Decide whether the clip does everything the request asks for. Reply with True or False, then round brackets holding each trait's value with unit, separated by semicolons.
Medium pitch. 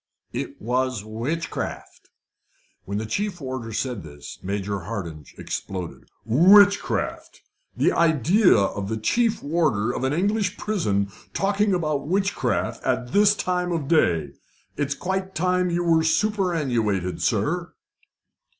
True (150 Hz)